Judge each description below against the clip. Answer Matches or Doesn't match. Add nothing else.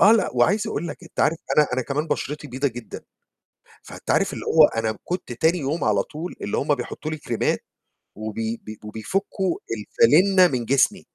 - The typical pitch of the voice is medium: Matches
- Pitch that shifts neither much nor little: Doesn't match